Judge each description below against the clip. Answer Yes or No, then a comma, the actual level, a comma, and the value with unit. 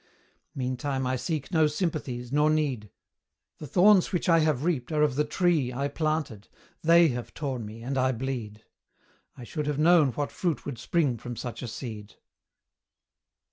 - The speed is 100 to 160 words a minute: No, average, 170 wpm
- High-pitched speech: No, medium, 140 Hz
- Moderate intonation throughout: Yes, average, 4.0 semitones